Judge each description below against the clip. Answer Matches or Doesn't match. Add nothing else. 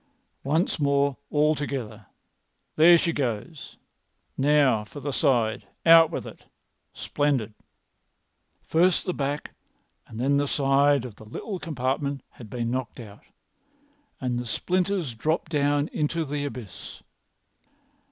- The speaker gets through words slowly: Matches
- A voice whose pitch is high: Doesn't match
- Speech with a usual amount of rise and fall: Matches